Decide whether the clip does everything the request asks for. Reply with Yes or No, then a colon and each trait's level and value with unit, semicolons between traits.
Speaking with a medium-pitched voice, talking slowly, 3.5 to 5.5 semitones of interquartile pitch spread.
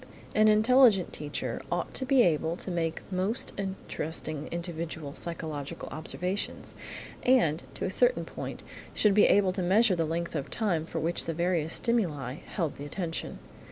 No: medium, 175 Hz; average, 155 wpm; average, 4.3 semitones